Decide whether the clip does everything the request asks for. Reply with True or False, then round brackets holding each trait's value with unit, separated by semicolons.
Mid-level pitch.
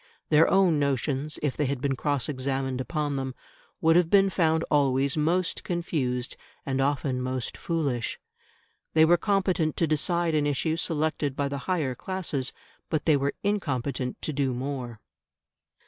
True (145 Hz)